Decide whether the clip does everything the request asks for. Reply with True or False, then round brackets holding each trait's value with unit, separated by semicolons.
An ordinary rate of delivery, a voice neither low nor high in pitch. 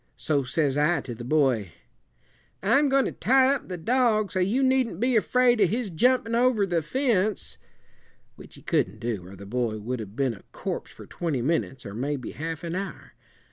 True (195 wpm; 170 Hz)